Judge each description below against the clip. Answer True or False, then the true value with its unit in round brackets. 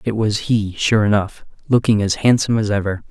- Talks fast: False (195 wpm)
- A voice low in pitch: True (105 Hz)